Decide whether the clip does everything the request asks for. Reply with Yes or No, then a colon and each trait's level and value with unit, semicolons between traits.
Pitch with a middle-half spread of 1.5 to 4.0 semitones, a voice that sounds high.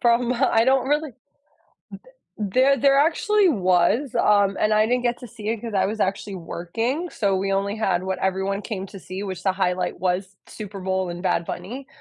No: average, 4.6 semitones; high, 205 Hz